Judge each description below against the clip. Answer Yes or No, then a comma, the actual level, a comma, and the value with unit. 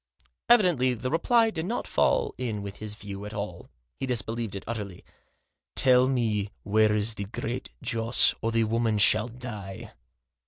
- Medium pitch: No, low, 115 Hz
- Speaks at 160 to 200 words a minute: Yes, average, 165 wpm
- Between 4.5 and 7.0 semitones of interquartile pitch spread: No, average, 3.5 semitones